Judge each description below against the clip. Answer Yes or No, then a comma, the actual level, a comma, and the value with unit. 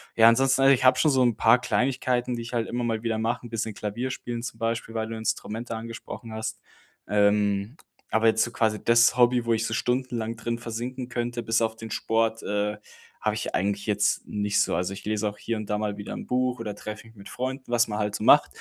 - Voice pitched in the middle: No, low, 115 Hz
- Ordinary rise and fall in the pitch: No, narrow, 2.1 semitones